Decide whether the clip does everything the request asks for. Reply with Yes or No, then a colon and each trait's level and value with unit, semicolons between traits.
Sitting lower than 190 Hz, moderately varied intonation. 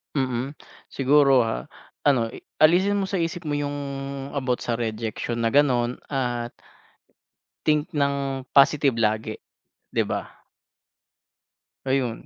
Yes: low, 135 Hz; average, 3.5 semitones